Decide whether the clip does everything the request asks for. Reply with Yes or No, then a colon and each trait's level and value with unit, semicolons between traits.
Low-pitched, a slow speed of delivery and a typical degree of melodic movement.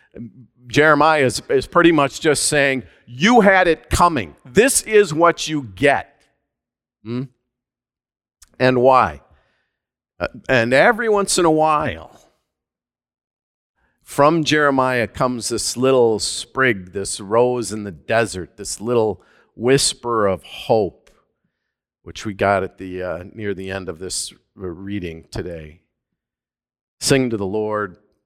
No: low, 120 Hz; slow, 125 wpm; wide, 6.4 semitones